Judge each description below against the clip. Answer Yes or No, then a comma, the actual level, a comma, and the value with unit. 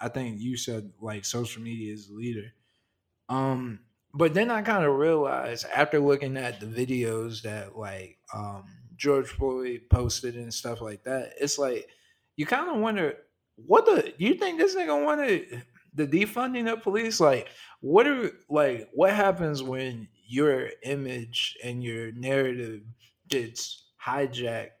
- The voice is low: Yes, low, 125 Hz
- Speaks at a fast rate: No, average, 150 wpm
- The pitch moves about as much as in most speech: No, wide, 6.1 semitones